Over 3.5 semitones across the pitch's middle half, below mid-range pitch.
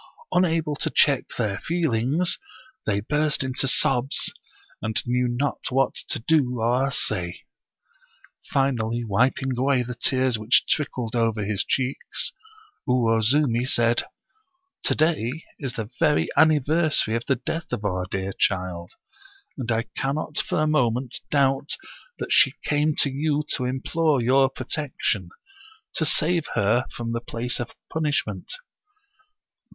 Yes: average, 4.4 semitones; low, 130 Hz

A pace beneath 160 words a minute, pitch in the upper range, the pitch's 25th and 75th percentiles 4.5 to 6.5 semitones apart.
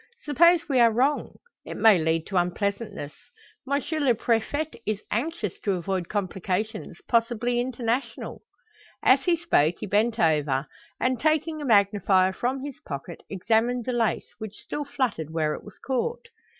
Yes: average, 150 wpm; high, 225 Hz; wide, 5.4 semitones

